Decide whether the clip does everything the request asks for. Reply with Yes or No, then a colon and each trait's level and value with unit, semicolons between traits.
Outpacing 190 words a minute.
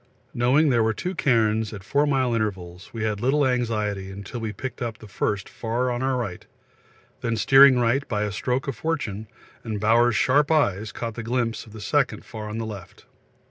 Yes: average, 200 wpm